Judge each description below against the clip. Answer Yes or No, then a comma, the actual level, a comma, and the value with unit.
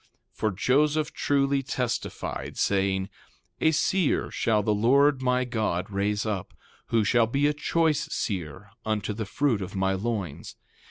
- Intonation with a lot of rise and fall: Yes, wide, 5.7 semitones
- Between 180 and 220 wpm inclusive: No, average, 150 wpm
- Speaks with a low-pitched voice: Yes, low, 115 Hz